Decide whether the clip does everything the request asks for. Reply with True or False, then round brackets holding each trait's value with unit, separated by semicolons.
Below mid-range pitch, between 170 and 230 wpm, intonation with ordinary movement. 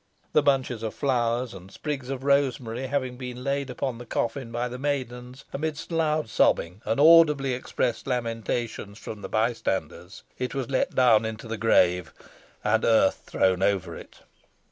False (125 Hz; 160 wpm; 3.5 semitones)